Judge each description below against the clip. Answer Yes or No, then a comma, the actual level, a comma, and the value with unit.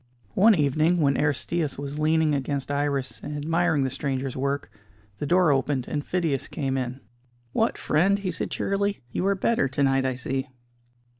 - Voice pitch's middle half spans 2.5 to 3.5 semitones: No, average, 4.0 semitones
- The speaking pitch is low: No, medium, 145 Hz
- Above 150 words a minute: Yes, average, 170 wpm